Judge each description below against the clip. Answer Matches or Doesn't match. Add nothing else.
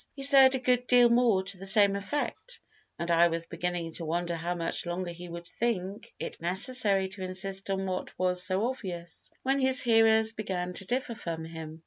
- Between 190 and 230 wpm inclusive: Matches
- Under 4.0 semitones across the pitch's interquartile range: Doesn't match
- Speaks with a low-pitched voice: Doesn't match